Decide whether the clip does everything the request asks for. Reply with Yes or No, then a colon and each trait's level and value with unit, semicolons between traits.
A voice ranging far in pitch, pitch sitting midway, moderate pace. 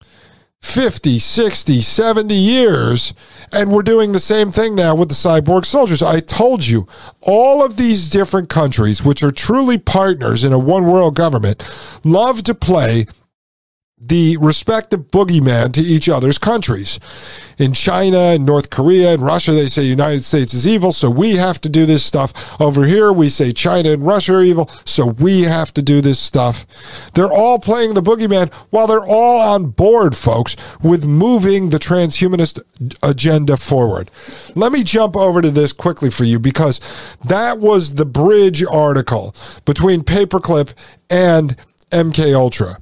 Yes: wide, 6.2 semitones; medium, 160 Hz; average, 160 wpm